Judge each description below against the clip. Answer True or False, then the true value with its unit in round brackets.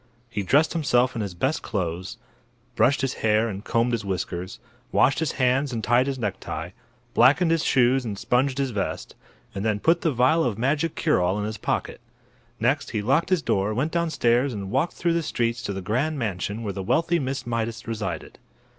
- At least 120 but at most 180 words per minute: False (200 wpm)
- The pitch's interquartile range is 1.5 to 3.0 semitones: False (5.1 semitones)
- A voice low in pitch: True (120 Hz)